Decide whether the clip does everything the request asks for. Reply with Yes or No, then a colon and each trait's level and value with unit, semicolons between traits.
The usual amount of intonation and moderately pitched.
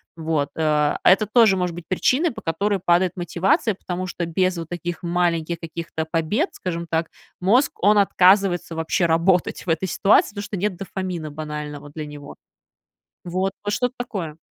Yes: average, 3.1 semitones; medium, 175 Hz